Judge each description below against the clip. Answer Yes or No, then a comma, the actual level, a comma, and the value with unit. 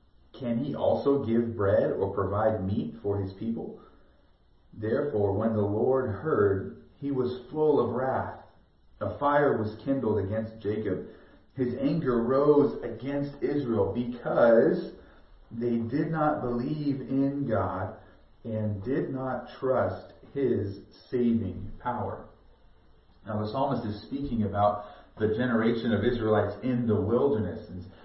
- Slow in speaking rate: Yes, slow, 125 wpm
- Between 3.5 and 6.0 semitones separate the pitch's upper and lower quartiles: Yes, average, 3.9 semitones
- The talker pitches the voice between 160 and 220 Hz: No, low, 115 Hz